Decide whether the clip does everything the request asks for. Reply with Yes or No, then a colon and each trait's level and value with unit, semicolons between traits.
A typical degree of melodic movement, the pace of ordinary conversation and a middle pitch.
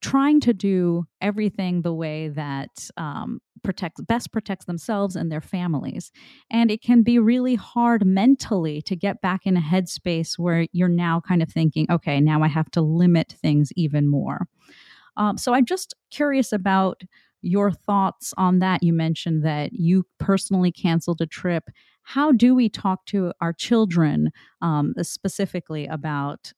Yes: average, 4.0 semitones; average, 160 wpm; medium, 180 Hz